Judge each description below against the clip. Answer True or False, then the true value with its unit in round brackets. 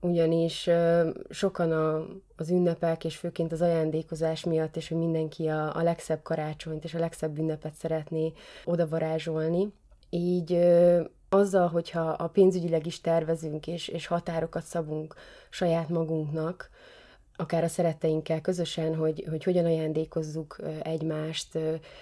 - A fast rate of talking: False (115 wpm)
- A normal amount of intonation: False (1.3 semitones)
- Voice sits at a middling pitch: True (165 Hz)